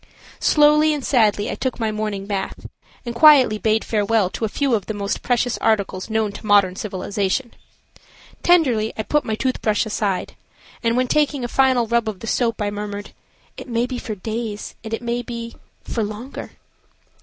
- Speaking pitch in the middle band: No, high, 225 Hz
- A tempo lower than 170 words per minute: No, average, 180 wpm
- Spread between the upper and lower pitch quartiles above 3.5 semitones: No, average, 2.9 semitones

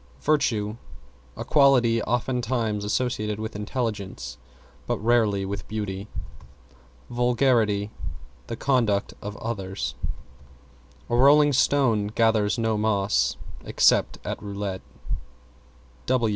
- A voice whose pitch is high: No, low, 110 Hz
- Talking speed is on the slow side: Yes, slow, 90 wpm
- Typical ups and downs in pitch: Yes, average, 3.0 semitones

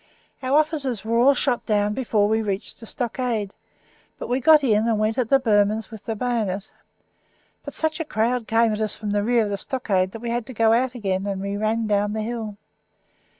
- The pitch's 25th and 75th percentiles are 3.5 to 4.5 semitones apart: No, average, 2.9 semitones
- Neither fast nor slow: No, fast, 220 wpm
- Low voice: No, high, 225 Hz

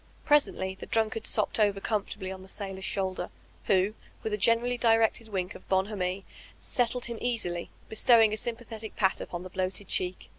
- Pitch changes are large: No, average, 3.2 semitones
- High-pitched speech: Yes, high, 210 Hz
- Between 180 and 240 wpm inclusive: No, average, 170 wpm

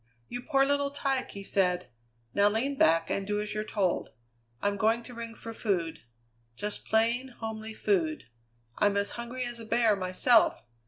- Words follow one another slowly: No, average, 170 wpm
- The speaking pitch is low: No, high, 220 Hz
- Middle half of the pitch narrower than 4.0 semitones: Yes, average, 3.4 semitones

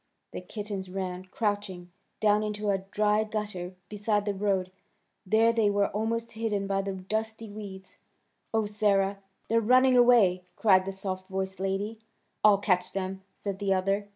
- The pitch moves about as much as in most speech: No, narrow, 2.0 semitones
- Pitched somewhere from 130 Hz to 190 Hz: No, high, 205 Hz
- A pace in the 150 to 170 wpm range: Yes, average, 155 wpm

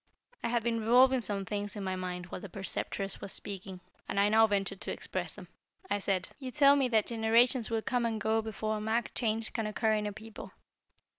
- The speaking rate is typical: No, fast, 220 wpm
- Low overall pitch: No, high, 220 Hz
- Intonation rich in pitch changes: No, average, 2.7 semitones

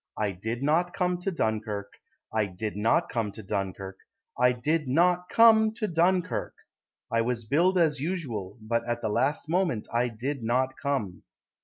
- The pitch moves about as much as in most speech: No, wide, 7.7 semitones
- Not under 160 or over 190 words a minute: Yes, average, 165 wpm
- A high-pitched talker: No, low, 125 Hz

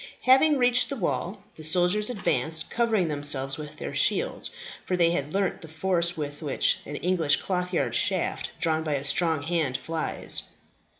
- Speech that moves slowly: No, average, 165 wpm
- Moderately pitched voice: Yes, medium, 165 Hz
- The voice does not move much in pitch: No, average, 3.9 semitones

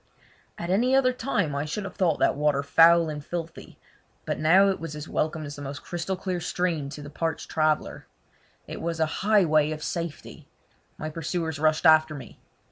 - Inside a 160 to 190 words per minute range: Yes, average, 185 wpm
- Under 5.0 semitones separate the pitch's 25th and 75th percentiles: Yes, narrow, 2.5 semitones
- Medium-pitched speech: Yes, medium, 160 Hz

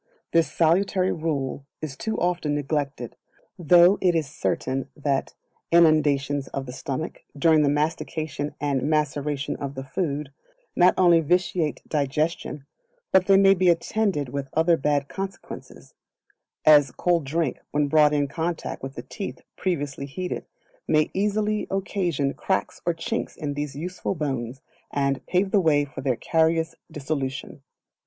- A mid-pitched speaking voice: Yes, medium, 155 Hz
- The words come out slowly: No, average, 145 wpm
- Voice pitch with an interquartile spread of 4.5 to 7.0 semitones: No, average, 3.7 semitones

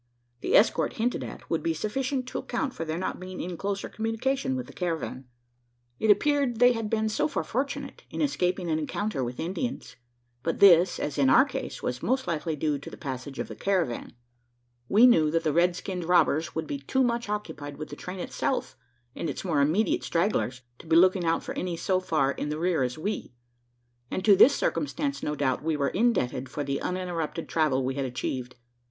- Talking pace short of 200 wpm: No, fast, 205 wpm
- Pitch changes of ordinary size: No, wide, 6.5 semitones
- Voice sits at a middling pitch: Yes, medium, 175 Hz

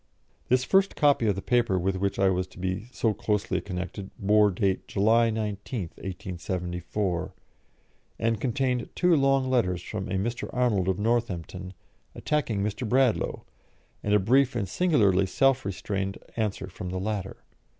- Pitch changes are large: No, average, 4.1 semitones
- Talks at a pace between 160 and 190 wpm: No, average, 150 wpm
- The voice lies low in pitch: Yes, low, 105 Hz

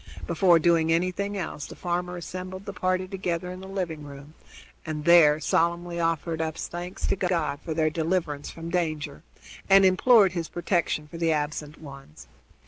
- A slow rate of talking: No, average, 165 wpm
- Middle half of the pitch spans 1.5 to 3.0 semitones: Yes, average, 2.7 semitones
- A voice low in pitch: No, medium, 170 Hz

